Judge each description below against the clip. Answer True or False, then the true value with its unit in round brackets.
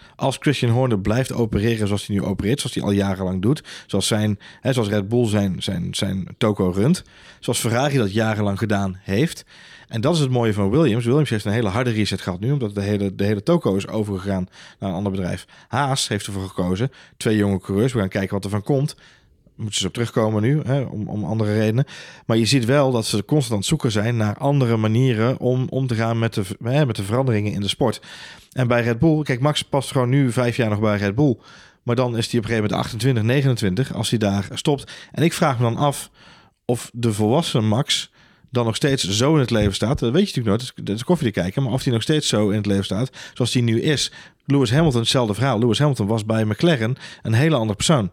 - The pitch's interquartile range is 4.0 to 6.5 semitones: True (4.4 semitones)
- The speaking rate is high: True (240 wpm)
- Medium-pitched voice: False (115 Hz)